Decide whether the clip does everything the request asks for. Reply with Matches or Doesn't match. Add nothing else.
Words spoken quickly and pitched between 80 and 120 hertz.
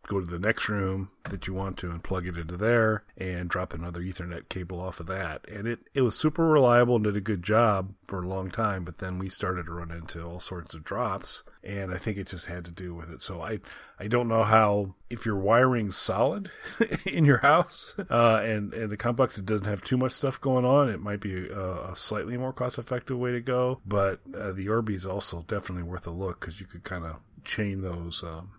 Matches